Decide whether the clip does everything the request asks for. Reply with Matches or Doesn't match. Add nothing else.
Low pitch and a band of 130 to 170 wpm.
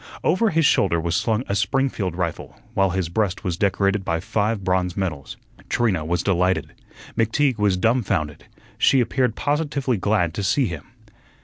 Matches